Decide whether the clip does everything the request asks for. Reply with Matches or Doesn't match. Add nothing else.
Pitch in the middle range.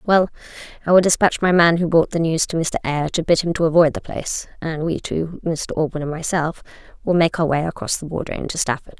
Matches